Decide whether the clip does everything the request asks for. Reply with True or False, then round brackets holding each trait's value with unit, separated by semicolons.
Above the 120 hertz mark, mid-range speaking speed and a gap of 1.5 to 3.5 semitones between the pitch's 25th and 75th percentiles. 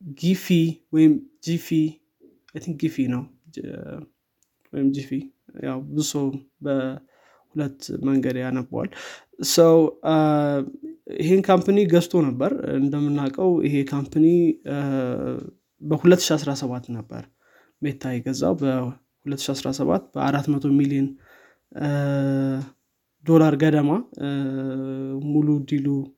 False (140 Hz; 65 wpm; 2.7 semitones)